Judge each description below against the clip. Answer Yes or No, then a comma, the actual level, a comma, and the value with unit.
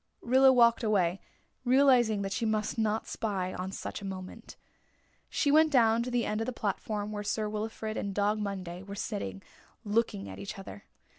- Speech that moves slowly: No, average, 180 wpm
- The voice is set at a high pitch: Yes, high, 215 Hz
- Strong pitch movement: No, average, 3.0 semitones